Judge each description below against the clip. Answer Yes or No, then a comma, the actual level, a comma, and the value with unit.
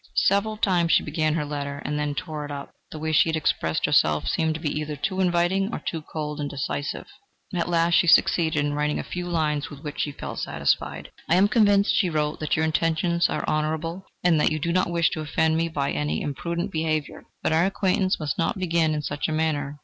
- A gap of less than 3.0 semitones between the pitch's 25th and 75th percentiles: Yes, narrow, 2.6 semitones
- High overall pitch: No, medium, 160 Hz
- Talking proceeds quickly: Yes, fast, 225 wpm